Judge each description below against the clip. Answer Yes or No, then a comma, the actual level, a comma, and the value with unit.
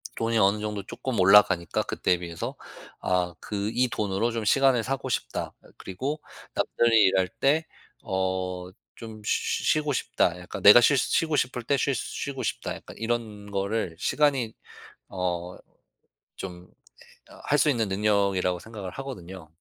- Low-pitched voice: Yes, low, 105 Hz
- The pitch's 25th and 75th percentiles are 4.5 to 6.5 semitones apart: Yes, average, 5.1 semitones